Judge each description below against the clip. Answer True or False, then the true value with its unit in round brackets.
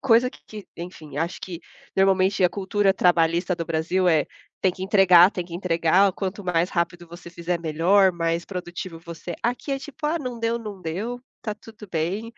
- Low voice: False (185 Hz)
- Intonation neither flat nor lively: True (3.3 semitones)